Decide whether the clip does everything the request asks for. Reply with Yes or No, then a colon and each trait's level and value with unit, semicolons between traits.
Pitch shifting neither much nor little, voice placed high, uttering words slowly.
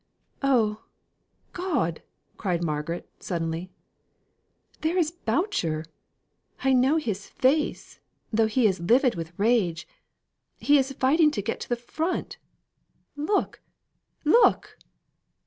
No: wide, 8.9 semitones; high, 240 Hz; slow, 110 wpm